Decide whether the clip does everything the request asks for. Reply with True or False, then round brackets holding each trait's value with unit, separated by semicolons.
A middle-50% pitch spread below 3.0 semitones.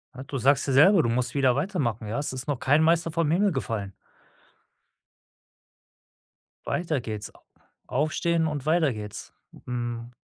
False (4.9 semitones)